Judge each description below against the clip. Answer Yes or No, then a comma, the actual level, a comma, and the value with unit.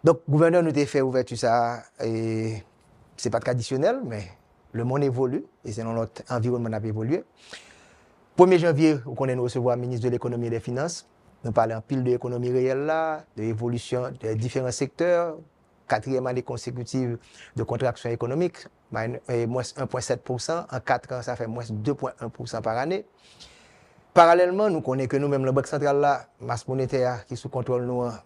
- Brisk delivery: No, average, 170 wpm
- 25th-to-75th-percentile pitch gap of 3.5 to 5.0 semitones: No, average, 2.9 semitones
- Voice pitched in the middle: No, low, 125 Hz